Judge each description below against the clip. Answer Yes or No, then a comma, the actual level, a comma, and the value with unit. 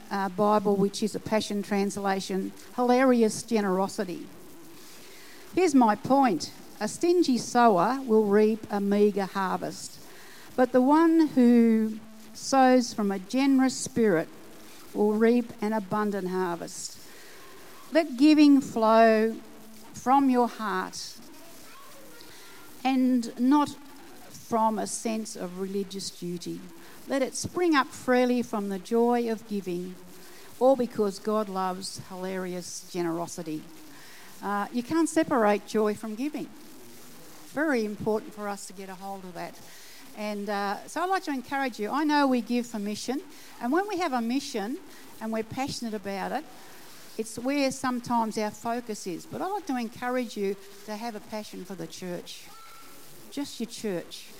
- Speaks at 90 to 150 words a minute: Yes, average, 140 wpm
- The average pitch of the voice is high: Yes, high, 225 Hz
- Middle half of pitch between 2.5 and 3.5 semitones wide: No, average, 4.6 semitones